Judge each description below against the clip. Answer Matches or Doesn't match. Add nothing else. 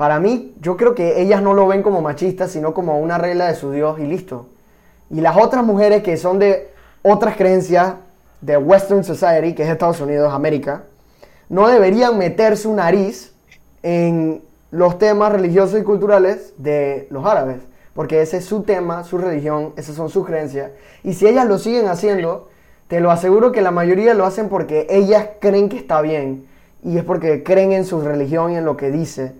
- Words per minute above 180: Matches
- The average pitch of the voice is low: Doesn't match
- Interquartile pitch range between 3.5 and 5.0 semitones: Matches